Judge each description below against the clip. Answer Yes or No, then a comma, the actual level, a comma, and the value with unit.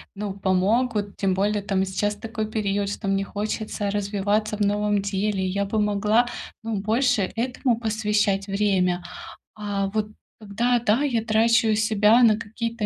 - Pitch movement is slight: Yes, narrow, 1.7 semitones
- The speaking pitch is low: No, high, 210 Hz